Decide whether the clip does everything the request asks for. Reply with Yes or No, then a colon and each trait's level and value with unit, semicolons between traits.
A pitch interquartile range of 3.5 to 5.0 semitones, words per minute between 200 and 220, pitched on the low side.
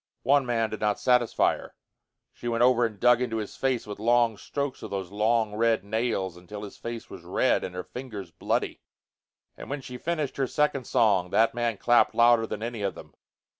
No: average, 2.7 semitones; fast, 205 wpm; low, 115 Hz